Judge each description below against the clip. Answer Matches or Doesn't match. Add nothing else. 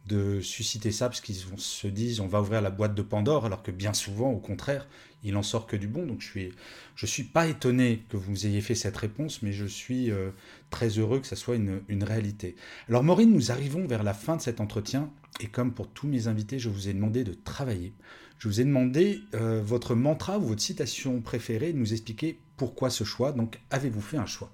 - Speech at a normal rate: Doesn't match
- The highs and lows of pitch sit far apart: Doesn't match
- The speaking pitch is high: Doesn't match